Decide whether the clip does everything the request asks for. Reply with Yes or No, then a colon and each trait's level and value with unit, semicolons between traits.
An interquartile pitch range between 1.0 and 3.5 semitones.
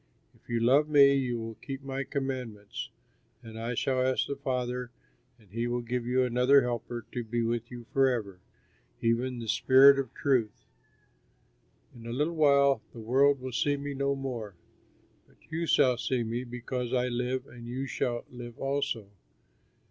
Yes: narrow, 2.5 semitones